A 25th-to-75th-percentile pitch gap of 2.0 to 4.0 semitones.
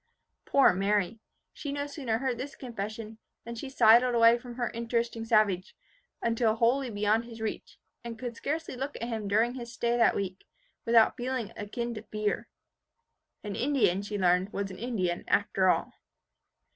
Yes: narrow, 2.6 semitones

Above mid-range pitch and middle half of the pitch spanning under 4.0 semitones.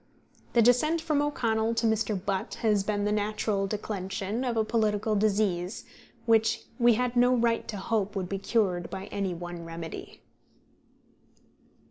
Yes: high, 215 Hz; average, 2.9 semitones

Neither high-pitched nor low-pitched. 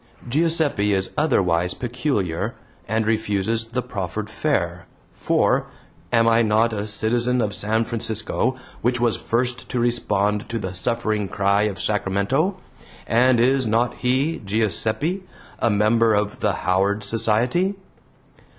No: low, 110 Hz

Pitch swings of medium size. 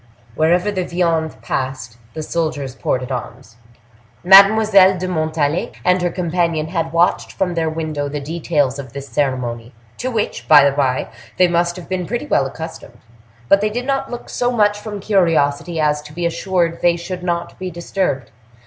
Yes: average, 4.2 semitones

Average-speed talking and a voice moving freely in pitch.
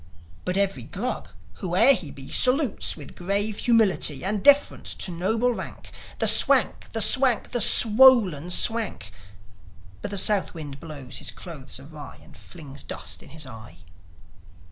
Yes: average, 145 wpm; wide, 7.2 semitones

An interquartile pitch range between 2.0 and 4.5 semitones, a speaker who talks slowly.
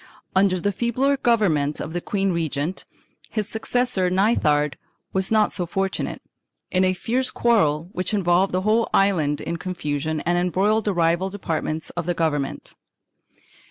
No: average, 4.0 semitones; average, 155 wpm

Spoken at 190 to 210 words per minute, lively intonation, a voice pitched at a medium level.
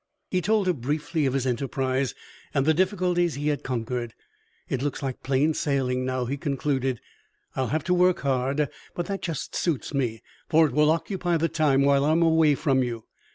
No: average, 200 wpm; average, 3.7 semitones; medium, 145 Hz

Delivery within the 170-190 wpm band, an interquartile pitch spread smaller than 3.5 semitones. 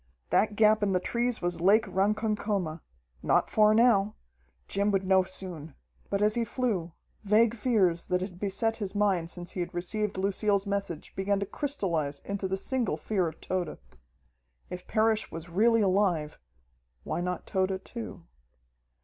No: average, 160 wpm; average, 3.0 semitones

